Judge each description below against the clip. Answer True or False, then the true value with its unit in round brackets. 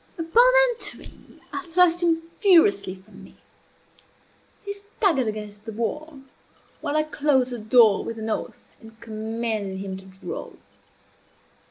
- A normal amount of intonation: False (7.4 semitones)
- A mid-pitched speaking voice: False (235 Hz)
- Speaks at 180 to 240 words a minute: False (135 wpm)